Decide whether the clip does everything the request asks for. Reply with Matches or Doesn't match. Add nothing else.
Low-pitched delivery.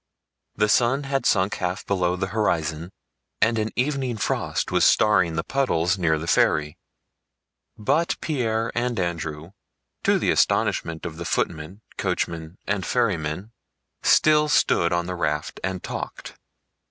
Matches